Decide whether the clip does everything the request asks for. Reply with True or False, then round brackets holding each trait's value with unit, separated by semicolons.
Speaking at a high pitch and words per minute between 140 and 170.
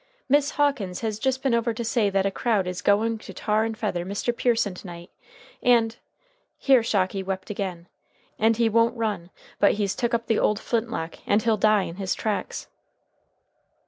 False (215 Hz; 190 wpm)